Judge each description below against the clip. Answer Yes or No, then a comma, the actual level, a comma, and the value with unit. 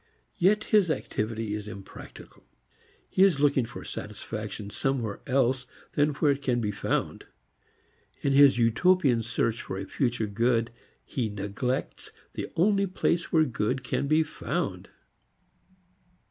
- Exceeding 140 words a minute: No, slow, 135 wpm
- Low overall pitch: Yes, low, 125 Hz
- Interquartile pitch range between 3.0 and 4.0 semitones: No, average, 5.1 semitones